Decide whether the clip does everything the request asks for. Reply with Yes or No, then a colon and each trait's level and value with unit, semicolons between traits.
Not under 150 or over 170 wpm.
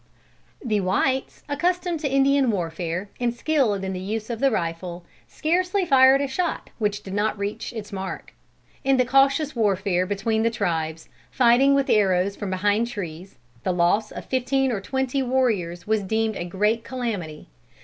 Yes: average, 165 wpm